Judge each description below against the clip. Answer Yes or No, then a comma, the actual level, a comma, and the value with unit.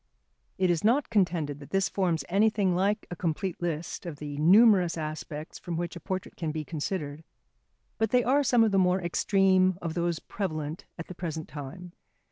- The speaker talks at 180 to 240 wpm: Yes, average, 185 wpm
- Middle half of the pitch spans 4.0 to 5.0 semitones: No, average, 3.5 semitones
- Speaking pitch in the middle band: Yes, medium, 175 Hz